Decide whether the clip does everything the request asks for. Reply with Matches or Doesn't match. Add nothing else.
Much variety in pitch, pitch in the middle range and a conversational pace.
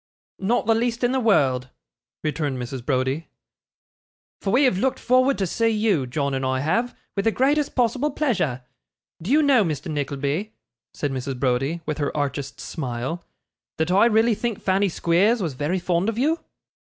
Matches